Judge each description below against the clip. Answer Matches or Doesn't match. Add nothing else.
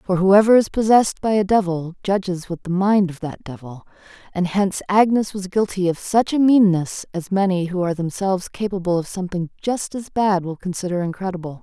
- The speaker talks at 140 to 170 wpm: Doesn't match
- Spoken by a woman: Matches